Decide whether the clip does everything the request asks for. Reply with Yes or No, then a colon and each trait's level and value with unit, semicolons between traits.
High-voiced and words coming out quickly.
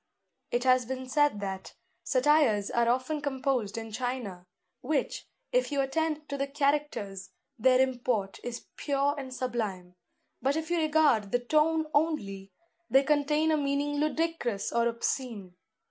No: very high, 260 Hz; average, 145 wpm